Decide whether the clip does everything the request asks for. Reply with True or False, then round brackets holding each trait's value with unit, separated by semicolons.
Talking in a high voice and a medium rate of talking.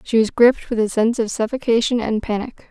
False (230 Hz; 220 wpm)